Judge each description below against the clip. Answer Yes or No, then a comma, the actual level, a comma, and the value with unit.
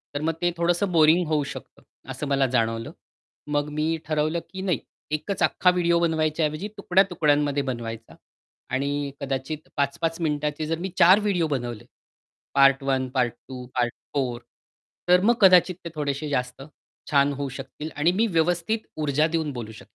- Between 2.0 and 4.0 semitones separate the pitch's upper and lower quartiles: Yes, average, 3.7 semitones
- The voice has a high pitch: No, medium, 150 Hz